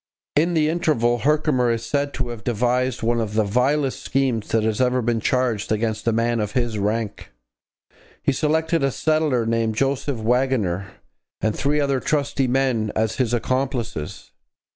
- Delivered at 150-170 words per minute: Yes, average, 165 wpm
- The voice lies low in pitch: Yes, low, 125 Hz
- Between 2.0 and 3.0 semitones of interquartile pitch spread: No, average, 3.5 semitones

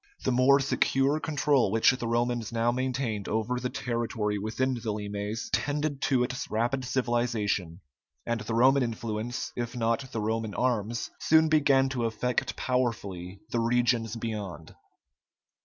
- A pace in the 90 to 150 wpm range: Yes, average, 140 wpm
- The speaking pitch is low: Yes, low, 120 Hz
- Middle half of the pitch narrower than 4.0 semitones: Yes, average, 2.8 semitones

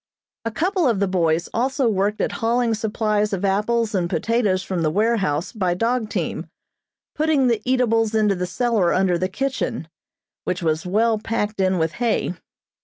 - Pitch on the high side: Yes, high, 210 Hz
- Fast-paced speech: No, average, 170 wpm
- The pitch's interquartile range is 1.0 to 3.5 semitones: No, average, 4.0 semitones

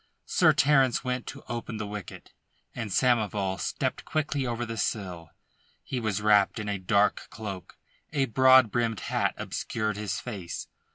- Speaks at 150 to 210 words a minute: Yes, average, 155 wpm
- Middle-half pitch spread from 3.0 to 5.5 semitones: Yes, average, 3.4 semitones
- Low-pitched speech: Yes, low, 110 Hz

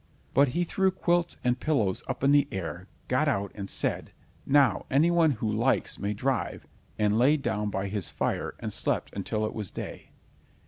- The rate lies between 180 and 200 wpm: Yes, average, 185 wpm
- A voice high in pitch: No, low, 125 Hz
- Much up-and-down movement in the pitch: Yes, wide, 5.7 semitones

